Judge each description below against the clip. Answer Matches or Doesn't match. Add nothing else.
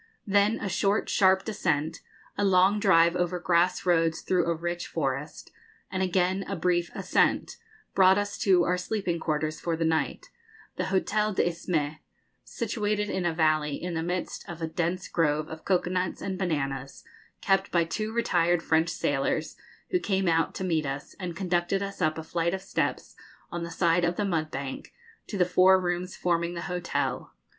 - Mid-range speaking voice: Matches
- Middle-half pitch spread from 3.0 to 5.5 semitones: Doesn't match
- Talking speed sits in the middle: Matches